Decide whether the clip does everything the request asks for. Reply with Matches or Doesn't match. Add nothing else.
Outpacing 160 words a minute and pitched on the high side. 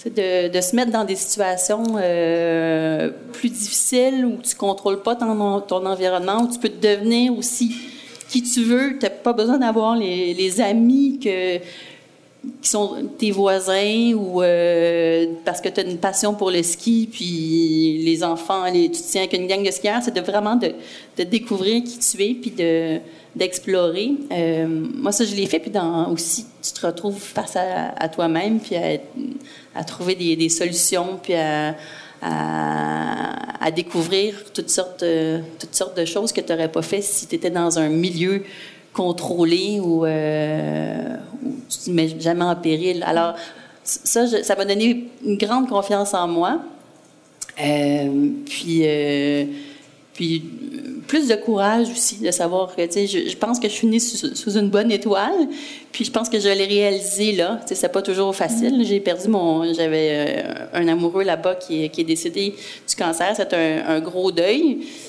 Matches